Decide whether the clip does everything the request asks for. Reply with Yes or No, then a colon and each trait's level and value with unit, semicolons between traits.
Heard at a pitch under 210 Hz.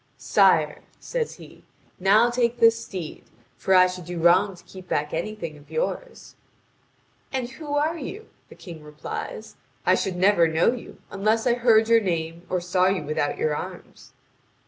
Yes: high, 190 Hz